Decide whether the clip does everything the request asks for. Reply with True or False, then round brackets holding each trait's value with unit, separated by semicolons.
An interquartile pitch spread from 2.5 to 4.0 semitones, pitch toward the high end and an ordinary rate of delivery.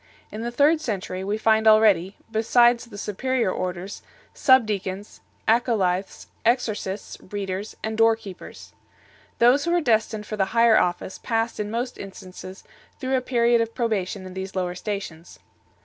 True (3.7 semitones; 215 Hz; 155 wpm)